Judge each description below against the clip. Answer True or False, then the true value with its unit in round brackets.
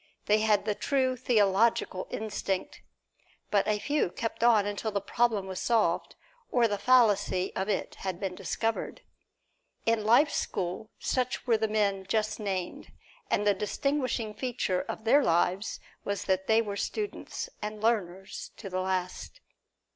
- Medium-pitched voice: False (210 Hz)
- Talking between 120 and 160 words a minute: True (150 wpm)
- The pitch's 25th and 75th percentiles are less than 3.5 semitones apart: True (3.1 semitones)